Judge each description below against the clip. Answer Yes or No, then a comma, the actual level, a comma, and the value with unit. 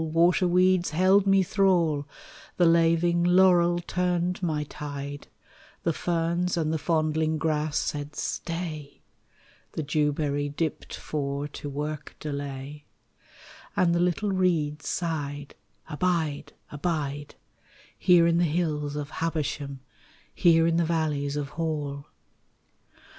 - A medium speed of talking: No, slow, 115 wpm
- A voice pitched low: No, medium, 160 Hz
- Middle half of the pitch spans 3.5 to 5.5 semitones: No, average, 2.8 semitones